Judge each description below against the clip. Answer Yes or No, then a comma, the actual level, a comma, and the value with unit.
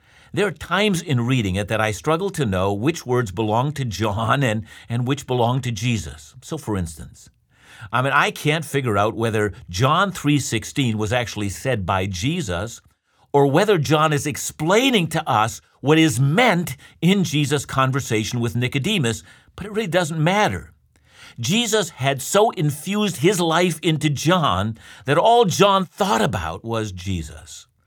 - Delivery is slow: No, average, 160 wpm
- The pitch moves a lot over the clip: Yes, wide, 7.3 semitones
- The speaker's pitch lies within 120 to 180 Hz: Yes, low, 135 Hz